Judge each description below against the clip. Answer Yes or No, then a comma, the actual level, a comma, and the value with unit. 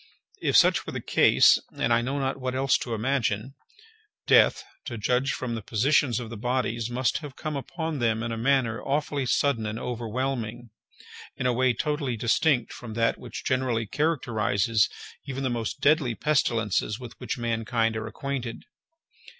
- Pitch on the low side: Yes, low, 120 Hz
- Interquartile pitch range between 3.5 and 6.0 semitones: No, average, 3.0 semitones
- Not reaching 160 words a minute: No, average, 165 wpm